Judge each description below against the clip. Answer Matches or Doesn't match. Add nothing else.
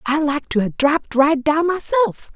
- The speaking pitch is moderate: Doesn't match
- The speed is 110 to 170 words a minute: Doesn't match